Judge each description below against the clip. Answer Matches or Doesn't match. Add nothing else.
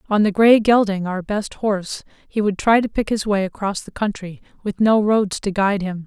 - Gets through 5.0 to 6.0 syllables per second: Matches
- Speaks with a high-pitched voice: Matches